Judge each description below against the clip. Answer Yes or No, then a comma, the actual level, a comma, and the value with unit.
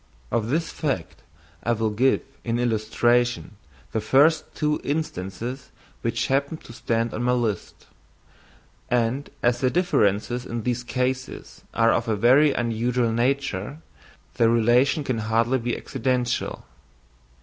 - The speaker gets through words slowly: Yes, slow, 130 wpm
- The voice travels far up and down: No, narrow, 2.6 semitones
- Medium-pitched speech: No, low, 120 Hz